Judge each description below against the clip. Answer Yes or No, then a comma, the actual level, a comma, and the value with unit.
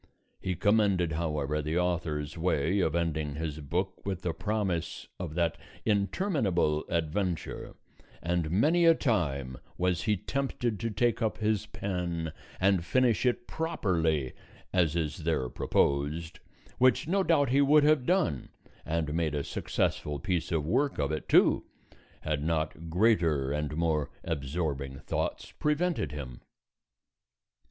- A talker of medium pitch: No, very low, 85 Hz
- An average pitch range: No, wide, 5.8 semitones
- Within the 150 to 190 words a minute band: No, slow, 135 wpm